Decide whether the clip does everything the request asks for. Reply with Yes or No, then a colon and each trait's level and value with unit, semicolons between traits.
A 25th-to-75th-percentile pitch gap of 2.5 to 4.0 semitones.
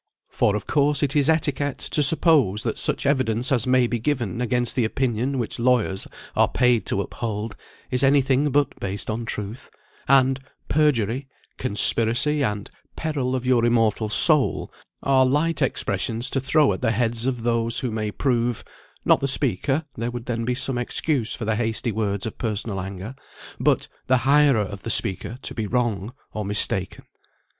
Yes: average, 3.5 semitones